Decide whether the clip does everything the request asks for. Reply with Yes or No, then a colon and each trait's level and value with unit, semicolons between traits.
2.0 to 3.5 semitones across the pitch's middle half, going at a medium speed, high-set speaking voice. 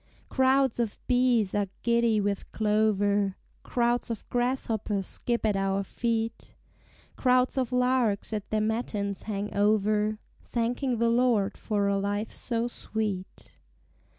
No: average, 2.9 semitones; slow, 125 wpm; high, 220 Hz